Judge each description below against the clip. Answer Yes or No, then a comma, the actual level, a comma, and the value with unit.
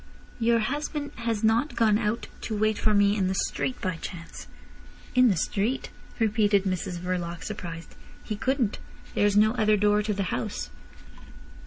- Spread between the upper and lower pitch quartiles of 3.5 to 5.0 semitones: No, average, 3.1 semitones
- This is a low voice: No, high, 210 Hz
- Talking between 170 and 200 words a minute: No, average, 160 wpm